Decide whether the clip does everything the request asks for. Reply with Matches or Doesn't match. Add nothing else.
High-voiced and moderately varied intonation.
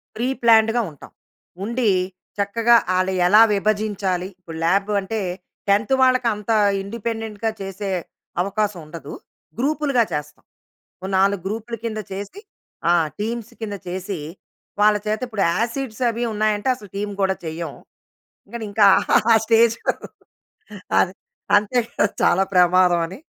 Matches